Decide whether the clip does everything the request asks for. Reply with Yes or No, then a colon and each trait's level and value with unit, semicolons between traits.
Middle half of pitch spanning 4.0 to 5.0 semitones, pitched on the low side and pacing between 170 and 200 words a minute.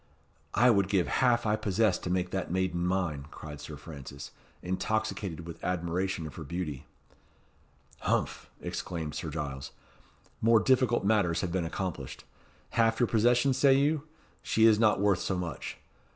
No: average, 4.7 semitones; very low, 95 Hz; average, 150 wpm